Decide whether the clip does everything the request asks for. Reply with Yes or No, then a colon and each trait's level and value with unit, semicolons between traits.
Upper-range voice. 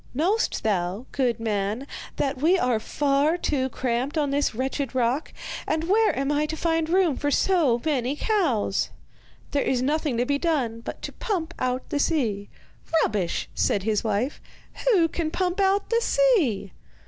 Yes: very high, 280 Hz